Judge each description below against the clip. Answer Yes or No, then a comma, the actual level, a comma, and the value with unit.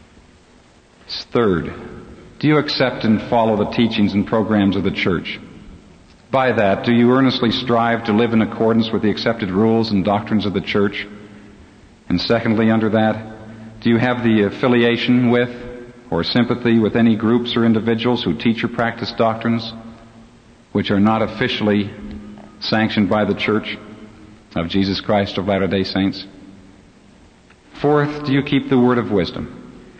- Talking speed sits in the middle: Yes, average, 150 wpm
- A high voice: No, low, 110 Hz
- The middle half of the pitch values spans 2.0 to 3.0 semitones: Yes, narrow, 2.5 semitones